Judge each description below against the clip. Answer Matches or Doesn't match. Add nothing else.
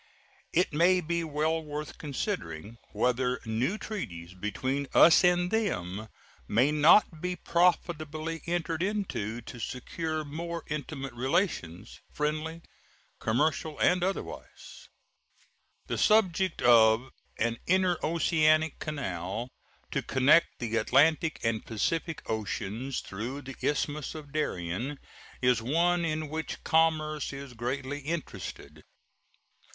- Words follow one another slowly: Matches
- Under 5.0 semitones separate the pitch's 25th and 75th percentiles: Doesn't match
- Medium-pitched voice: Matches